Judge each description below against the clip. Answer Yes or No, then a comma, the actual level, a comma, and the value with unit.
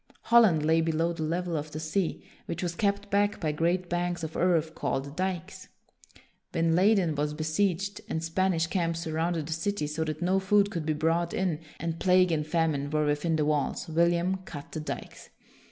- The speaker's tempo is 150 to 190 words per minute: Yes, average, 185 wpm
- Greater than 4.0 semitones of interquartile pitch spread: No, average, 2.8 semitones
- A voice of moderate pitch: Yes, medium, 165 Hz